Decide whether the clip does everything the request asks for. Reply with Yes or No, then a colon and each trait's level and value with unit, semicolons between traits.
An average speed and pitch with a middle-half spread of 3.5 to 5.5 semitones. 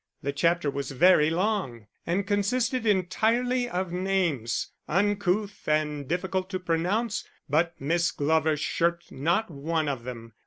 No: slow, 130 wpm; average, 4.8 semitones